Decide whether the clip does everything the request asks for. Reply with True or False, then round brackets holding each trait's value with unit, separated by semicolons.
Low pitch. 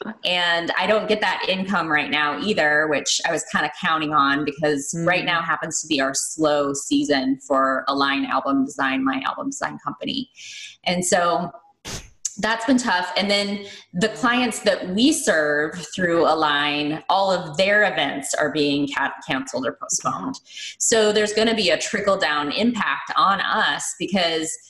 False (170 Hz)